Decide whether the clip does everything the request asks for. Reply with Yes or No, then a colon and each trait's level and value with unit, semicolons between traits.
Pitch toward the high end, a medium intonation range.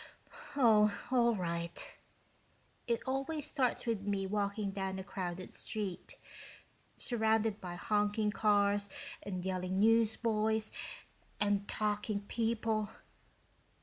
No: high, 210 Hz; narrow, 2.2 semitones